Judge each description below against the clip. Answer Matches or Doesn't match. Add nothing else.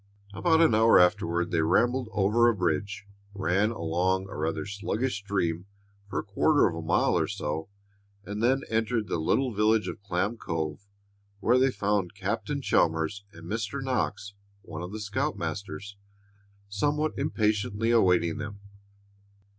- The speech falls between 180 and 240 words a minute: Doesn't match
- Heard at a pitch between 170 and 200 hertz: Doesn't match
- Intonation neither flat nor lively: Matches